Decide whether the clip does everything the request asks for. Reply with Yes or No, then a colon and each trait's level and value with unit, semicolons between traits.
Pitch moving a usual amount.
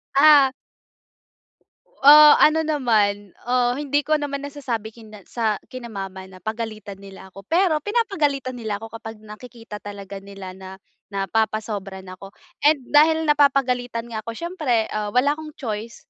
No: wide, 5.7 semitones